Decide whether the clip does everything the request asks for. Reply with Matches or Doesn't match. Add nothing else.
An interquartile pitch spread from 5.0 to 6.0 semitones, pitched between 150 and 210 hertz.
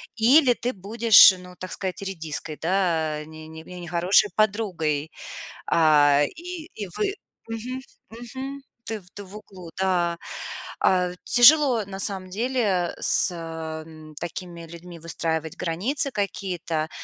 Matches